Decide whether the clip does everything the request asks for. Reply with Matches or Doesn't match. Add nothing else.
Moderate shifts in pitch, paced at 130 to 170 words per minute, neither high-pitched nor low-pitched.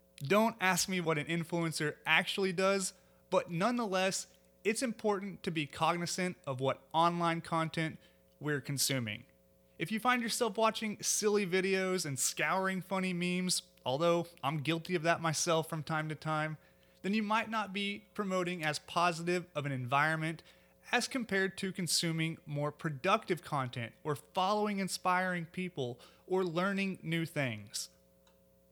Matches